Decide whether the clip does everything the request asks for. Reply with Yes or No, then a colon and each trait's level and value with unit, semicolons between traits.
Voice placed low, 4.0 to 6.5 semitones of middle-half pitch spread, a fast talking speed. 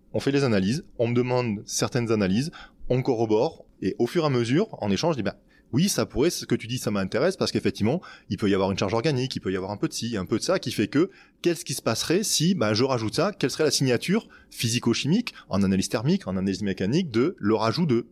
Yes: low, 120 Hz; wide, 5.5 semitones; fast, 260 wpm